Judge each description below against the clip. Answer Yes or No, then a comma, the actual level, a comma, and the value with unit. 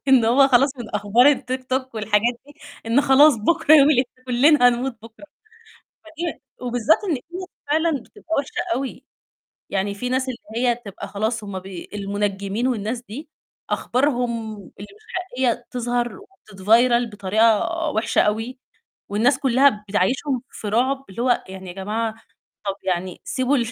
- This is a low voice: No, high, 240 Hz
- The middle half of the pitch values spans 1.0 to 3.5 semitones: No, average, 4.2 semitones